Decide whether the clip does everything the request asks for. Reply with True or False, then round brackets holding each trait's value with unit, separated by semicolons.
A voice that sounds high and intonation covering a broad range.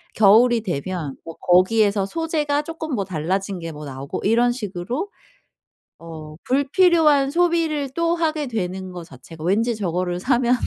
True (215 Hz; 8.3 semitones)